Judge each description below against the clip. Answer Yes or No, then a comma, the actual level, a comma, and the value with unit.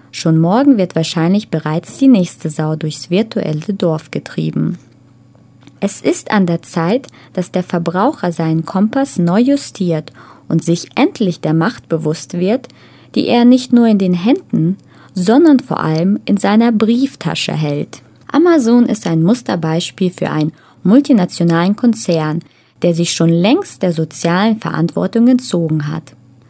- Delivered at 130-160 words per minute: Yes, average, 140 wpm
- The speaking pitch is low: No, medium, 175 Hz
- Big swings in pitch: Yes, wide, 6.1 semitones